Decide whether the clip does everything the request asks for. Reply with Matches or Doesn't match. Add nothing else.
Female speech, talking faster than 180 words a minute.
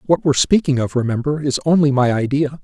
Doesn't match